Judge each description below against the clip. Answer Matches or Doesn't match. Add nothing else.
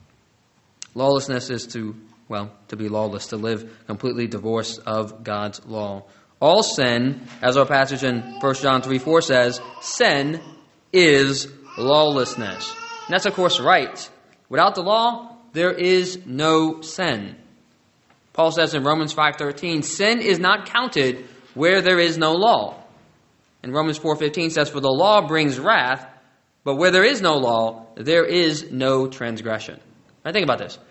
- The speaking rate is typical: Matches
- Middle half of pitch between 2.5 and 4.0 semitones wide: Doesn't match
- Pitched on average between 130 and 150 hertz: Matches